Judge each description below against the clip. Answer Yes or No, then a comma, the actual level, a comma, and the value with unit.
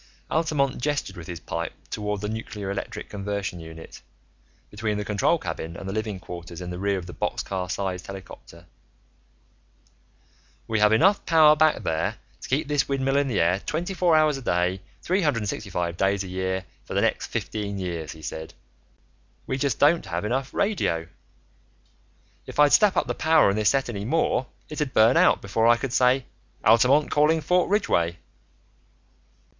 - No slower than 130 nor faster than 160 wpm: No, average, 180 wpm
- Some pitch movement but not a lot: No, wide, 7.6 semitones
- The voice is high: No, low, 105 Hz